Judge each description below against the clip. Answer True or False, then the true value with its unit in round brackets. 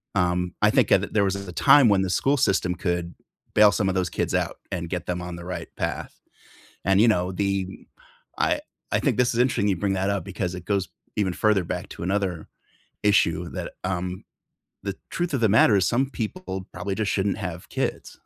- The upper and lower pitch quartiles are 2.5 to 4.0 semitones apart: True (2.8 semitones)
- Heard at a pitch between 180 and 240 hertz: False (95 Hz)